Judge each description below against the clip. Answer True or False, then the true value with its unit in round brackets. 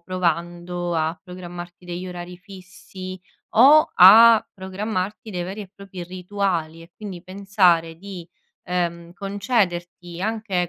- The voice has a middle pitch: True (180 Hz)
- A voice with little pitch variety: True (2.3 semitones)